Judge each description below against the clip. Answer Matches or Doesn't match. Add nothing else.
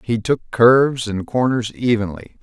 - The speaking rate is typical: Matches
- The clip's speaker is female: Doesn't match